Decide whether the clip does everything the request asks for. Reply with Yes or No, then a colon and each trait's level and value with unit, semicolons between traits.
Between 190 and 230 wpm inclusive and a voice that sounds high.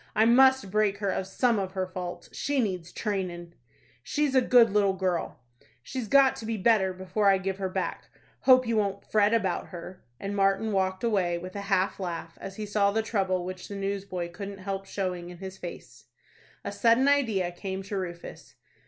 Yes: average, 195 wpm; high, 195 Hz